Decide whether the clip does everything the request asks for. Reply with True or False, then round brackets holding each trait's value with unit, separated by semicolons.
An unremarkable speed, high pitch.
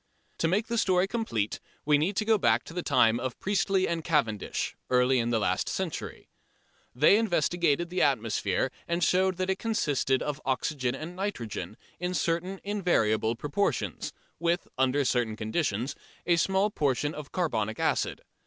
False (155 wpm; 150 Hz)